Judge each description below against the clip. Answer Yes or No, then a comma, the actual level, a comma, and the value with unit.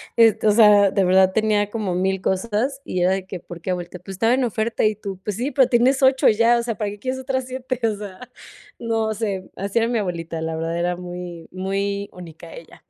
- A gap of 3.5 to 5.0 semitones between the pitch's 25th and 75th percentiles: Yes, average, 3.9 semitones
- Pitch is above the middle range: Yes, high, 205 Hz